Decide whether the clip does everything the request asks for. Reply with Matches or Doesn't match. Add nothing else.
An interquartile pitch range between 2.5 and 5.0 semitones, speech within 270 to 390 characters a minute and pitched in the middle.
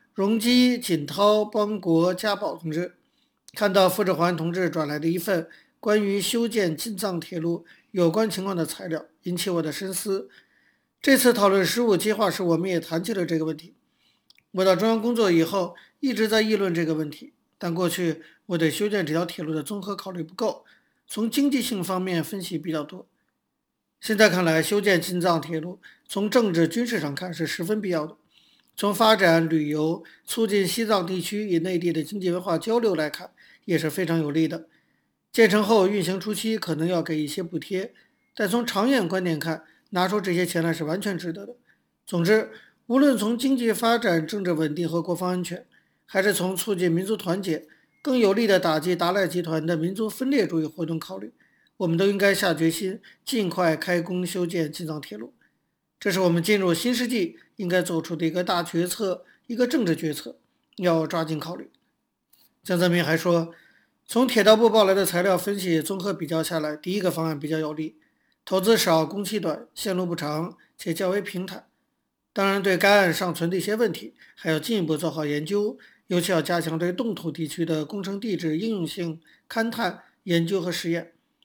Matches